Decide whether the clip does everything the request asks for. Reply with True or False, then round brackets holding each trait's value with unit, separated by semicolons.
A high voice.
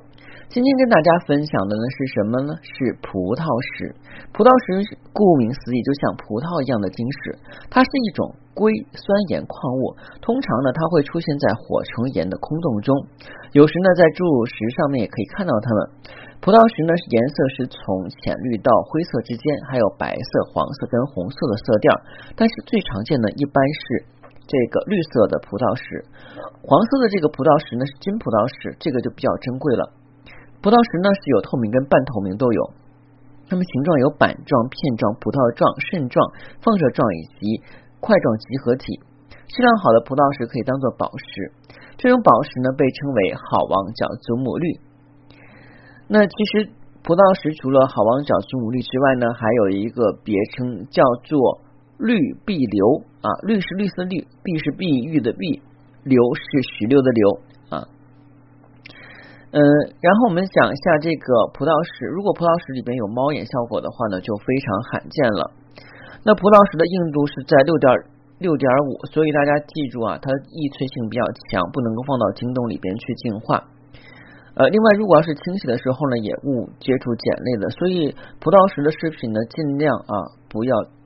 False (140 Hz)